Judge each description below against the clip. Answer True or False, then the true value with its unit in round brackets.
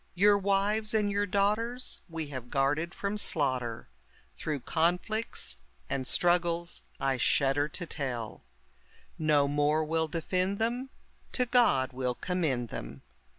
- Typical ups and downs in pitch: False (6.7 semitones)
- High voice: False (165 Hz)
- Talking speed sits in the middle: False (125 wpm)